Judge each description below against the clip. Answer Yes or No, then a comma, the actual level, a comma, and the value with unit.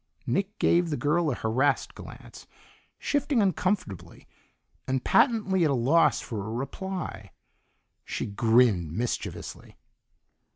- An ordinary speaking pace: No, slow, 115 wpm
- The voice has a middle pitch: Yes, medium, 145 Hz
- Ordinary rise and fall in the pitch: No, wide, 8.5 semitones